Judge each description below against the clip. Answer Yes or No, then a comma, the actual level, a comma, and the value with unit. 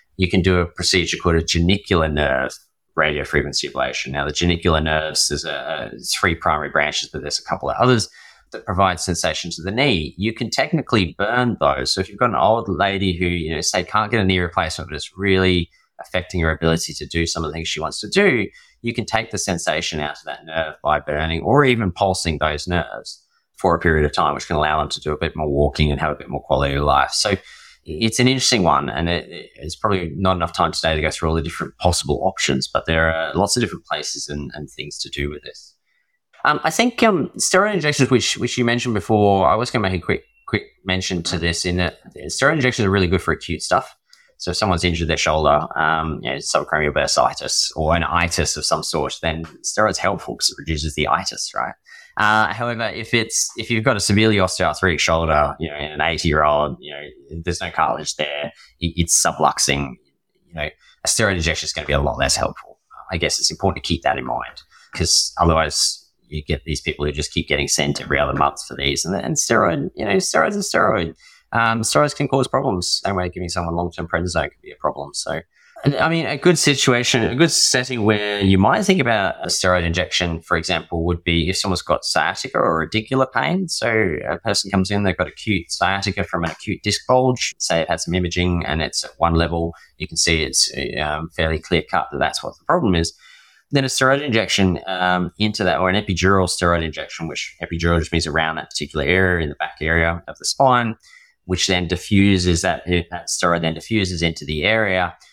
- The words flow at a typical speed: No, fast, 225 wpm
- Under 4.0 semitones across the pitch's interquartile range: No, average, 4.7 semitones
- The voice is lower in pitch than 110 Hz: Yes, very low, 90 Hz